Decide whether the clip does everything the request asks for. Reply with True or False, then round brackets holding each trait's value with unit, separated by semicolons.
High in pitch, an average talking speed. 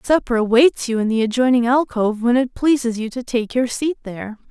False (245 Hz; 215 wpm)